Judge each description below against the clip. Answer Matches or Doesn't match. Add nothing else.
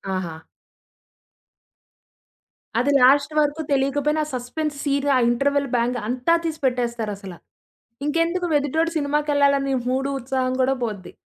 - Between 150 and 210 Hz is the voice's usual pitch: Doesn't match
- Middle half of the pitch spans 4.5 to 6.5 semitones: Doesn't match